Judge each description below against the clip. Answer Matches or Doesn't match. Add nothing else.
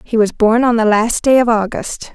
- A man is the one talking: Doesn't match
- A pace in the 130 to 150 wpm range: Doesn't match